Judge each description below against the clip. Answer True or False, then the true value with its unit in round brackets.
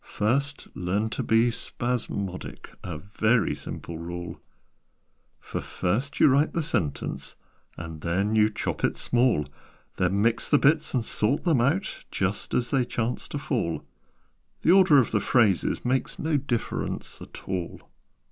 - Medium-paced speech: True (145 wpm)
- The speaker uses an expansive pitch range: True (6.6 semitones)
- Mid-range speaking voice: False (115 Hz)